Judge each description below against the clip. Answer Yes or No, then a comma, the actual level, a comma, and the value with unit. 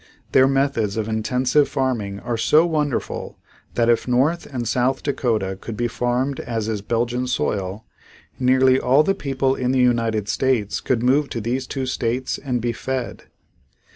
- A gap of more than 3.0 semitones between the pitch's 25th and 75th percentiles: No, narrow, 2.5 semitones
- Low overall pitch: Yes, low, 125 Hz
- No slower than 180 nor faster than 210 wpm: No, average, 165 wpm